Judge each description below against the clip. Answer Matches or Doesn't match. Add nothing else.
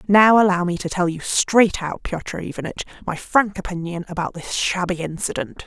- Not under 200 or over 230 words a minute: Doesn't match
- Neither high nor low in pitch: Matches